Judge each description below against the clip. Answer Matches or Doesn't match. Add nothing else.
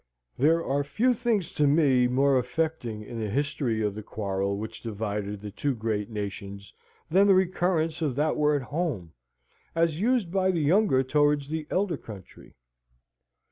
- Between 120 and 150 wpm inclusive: Doesn't match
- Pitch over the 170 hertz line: Doesn't match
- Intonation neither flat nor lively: Doesn't match